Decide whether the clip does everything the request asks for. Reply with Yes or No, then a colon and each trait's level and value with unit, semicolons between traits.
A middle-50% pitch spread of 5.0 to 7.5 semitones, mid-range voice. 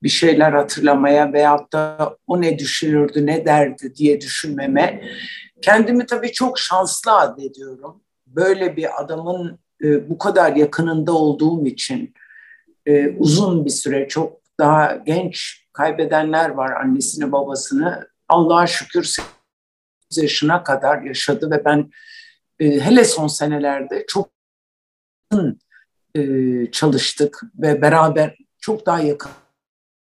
No: average, 4.3 semitones; medium, 155 Hz